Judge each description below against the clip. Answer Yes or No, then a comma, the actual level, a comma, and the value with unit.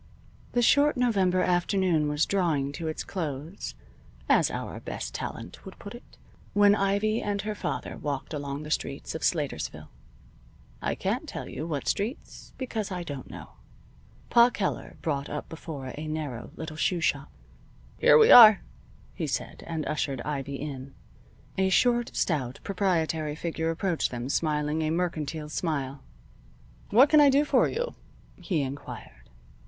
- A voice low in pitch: No, medium, 160 Hz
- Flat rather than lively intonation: No, wide, 5.4 semitones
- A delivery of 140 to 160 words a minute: Yes, average, 150 wpm